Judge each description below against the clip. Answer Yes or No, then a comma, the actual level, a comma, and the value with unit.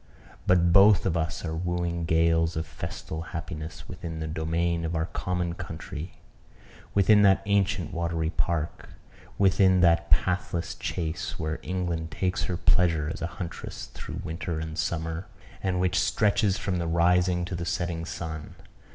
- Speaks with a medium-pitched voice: No, very low, 85 Hz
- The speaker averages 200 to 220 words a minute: No, average, 150 wpm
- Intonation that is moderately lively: No, narrow, 1.9 semitones